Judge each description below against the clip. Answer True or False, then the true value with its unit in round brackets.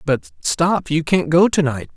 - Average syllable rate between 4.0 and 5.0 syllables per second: True (4.1 syllables/s)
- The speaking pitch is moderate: True (160 Hz)